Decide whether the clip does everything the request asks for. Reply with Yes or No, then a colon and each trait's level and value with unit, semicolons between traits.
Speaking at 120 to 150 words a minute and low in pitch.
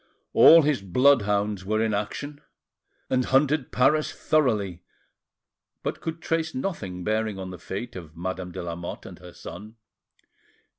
Yes: average, 140 wpm; low, 110 Hz